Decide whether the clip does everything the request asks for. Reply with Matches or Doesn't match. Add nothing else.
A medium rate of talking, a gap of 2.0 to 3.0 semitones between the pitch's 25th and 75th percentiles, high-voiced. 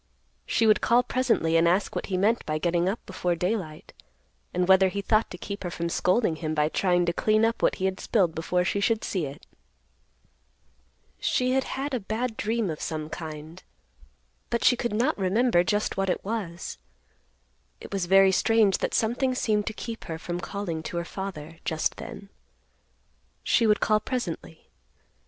Doesn't match